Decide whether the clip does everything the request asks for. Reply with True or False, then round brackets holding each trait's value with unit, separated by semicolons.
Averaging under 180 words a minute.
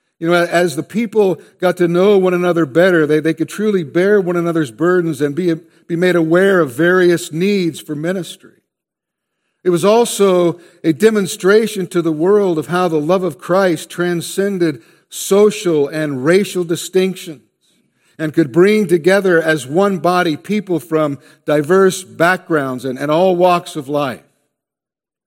True (155 wpm)